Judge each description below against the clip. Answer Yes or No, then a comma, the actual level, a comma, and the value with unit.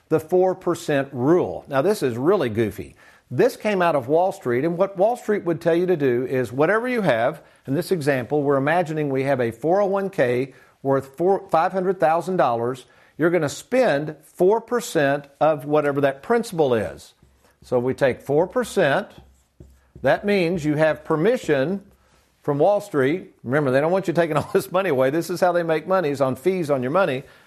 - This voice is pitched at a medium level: Yes, medium, 160 Hz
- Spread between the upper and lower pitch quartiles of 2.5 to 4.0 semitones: No, average, 5.3 semitones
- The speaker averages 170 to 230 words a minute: Yes, average, 175 wpm